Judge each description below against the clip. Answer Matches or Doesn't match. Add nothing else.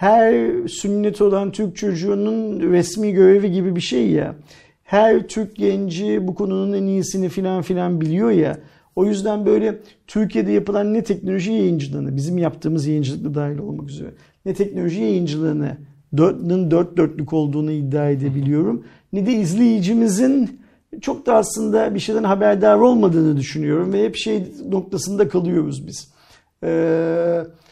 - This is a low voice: Doesn't match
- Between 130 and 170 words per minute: Matches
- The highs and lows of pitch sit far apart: Doesn't match